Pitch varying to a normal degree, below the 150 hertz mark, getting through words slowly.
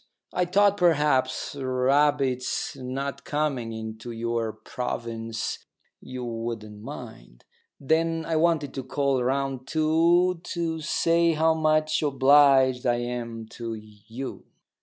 Yes: average, 4.8 semitones; low, 135 Hz; slow, 115 wpm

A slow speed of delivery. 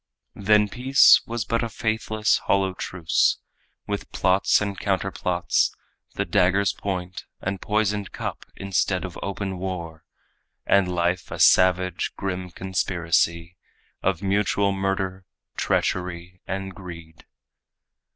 Yes: slow, 115 wpm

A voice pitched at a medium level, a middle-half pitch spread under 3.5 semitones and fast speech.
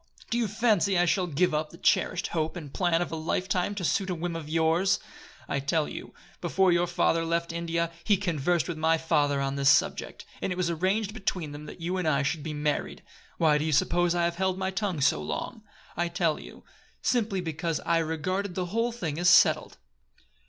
Yes: medium, 170 Hz; average, 2.9 semitones; fast, 215 wpm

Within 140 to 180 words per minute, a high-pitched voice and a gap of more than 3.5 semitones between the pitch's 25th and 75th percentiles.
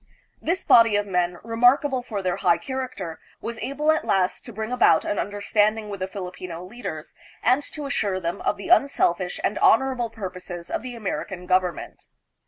Yes: average, 175 wpm; high, 205 Hz; average, 5.2 semitones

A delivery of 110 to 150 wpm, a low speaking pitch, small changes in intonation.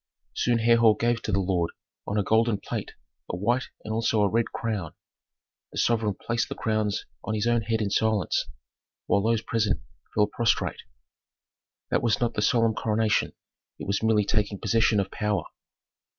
No: average, 170 wpm; low, 110 Hz; narrow, 2.0 semitones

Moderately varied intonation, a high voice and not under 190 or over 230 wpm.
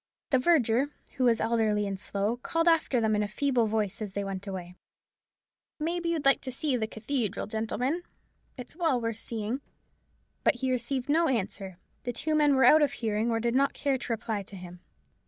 Yes: average, 4.6 semitones; high, 235 Hz; average, 195 wpm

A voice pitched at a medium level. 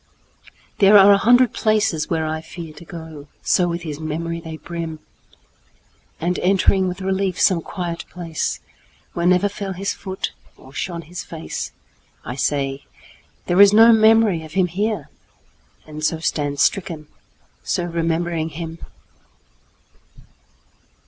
Yes: medium, 170 Hz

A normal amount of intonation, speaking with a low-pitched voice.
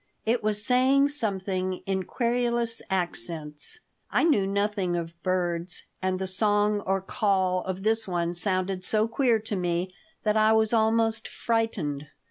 No: average, 3.5 semitones; high, 200 Hz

